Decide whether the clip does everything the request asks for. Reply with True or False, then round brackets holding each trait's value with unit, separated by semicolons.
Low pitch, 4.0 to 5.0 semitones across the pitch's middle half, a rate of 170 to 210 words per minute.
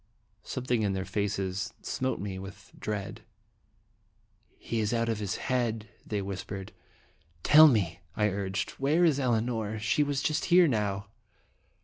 False (105 Hz; 4.4 semitones; 145 wpm)